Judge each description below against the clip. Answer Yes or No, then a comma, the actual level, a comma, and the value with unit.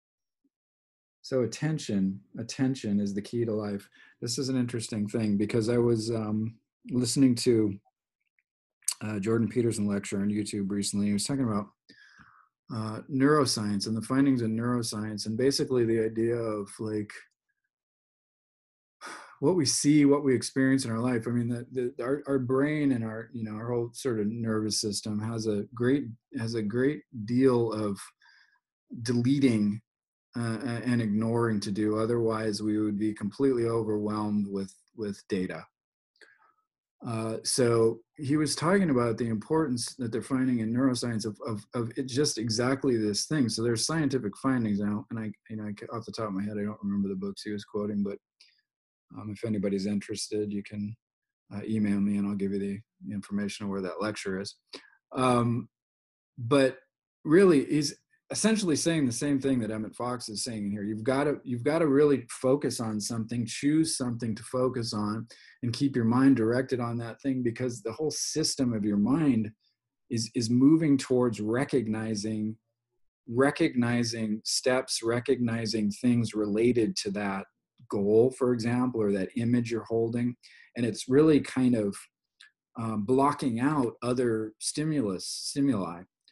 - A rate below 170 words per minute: Yes, average, 160 wpm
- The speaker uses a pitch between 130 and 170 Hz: No, low, 115 Hz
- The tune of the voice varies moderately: Yes, average, 3.5 semitones